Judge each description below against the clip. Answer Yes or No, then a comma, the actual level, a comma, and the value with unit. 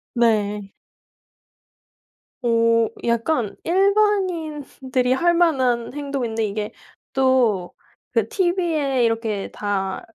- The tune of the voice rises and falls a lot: Yes, wide, 6.2 semitones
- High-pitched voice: Yes, very high, 250 Hz